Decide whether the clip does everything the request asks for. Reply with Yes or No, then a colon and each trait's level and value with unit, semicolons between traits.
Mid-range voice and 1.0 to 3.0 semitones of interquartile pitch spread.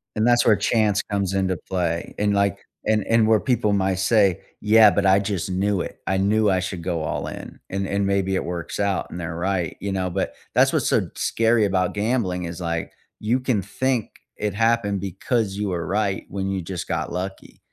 No: low, 100 Hz; narrow, 2.4 semitones